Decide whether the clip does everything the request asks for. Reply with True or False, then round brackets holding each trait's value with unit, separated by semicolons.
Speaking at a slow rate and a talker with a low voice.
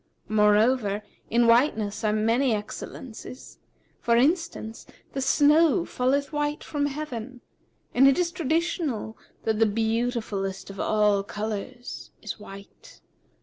False (110 wpm; 235 Hz)